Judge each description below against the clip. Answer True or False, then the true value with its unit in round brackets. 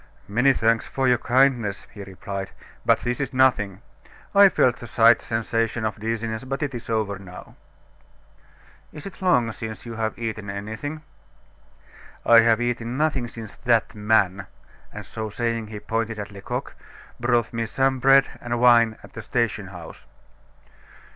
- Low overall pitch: True (115 Hz)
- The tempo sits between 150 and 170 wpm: True (155 wpm)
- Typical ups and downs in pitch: False (2.3 semitones)